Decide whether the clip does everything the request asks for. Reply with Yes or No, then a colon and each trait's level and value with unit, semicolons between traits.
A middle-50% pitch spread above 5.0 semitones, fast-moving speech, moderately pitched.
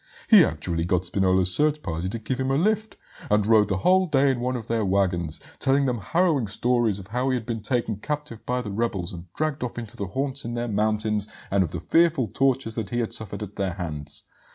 No: wide, 5.4 semitones; fast, 230 wpm; low, 115 Hz